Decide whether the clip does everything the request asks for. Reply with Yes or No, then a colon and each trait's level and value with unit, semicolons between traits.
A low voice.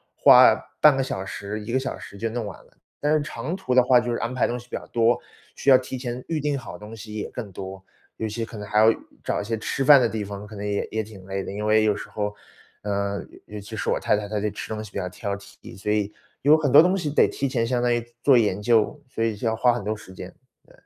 Yes: low, 110 Hz